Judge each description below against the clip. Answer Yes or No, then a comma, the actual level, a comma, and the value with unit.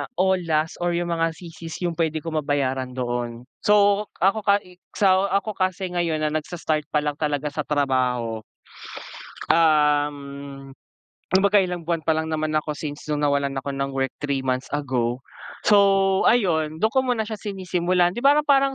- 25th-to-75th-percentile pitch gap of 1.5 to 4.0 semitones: No, average, 4.8 semitones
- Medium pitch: Yes, medium, 160 Hz